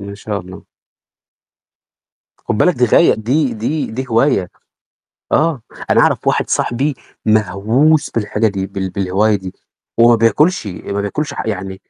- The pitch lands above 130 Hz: No, low, 110 Hz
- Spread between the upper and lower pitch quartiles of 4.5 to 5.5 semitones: Yes, average, 5.0 semitones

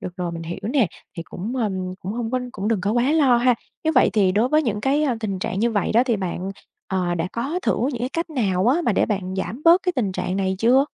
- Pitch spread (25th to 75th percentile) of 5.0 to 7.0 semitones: Yes, average, 5.3 semitones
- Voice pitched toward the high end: Yes, high, 220 Hz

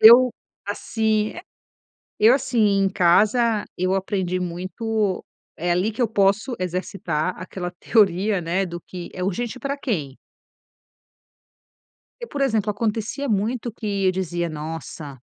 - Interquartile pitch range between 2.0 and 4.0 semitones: Yes, average, 3.7 semitones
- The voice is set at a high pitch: Yes, high, 200 Hz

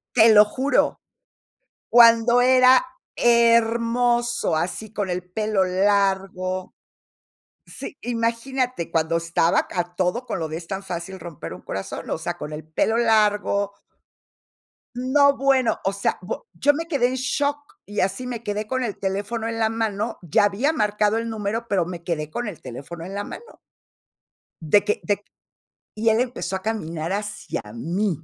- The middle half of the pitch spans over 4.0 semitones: Yes, average, 4.5 semitones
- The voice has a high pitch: Yes, high, 210 Hz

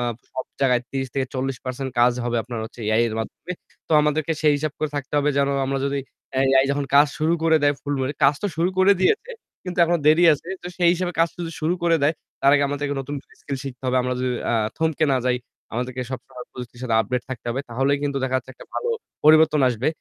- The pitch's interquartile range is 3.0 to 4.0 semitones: Yes, average, 3.4 semitones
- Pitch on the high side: No, medium, 140 Hz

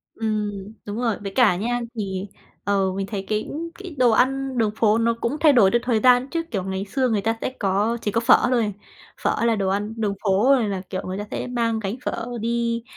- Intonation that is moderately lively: Yes, average, 3.0 semitones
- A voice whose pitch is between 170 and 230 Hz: Yes, high, 220 Hz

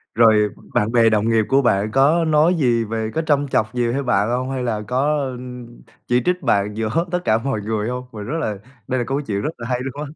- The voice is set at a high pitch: No, low, 120 Hz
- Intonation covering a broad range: No, average, 3.9 semitones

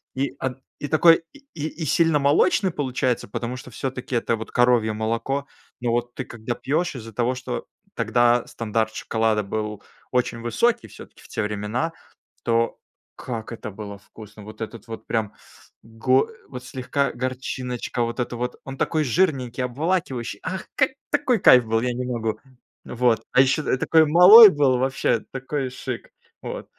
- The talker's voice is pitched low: Yes, low, 125 Hz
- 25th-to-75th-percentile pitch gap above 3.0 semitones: Yes, average, 3.5 semitones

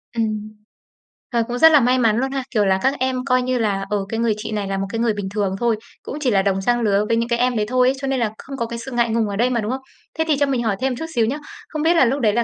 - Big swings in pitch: No, average, 3.2 semitones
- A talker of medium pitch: No, high, 235 Hz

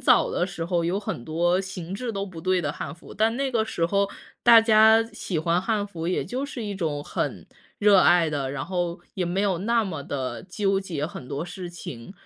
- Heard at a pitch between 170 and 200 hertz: Yes, medium, 185 Hz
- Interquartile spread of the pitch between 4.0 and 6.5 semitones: No, average, 3.6 semitones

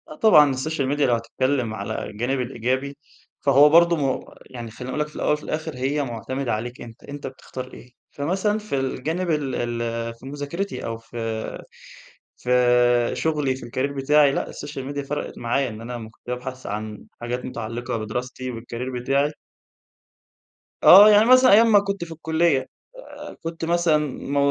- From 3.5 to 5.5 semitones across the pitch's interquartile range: Yes, average, 3.8 semitones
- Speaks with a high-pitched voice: No, low, 135 Hz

